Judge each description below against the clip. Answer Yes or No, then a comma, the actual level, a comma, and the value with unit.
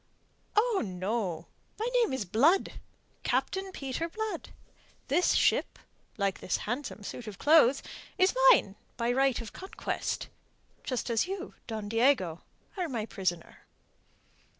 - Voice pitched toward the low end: No, very high, 250 Hz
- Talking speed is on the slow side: Yes, slow, 125 wpm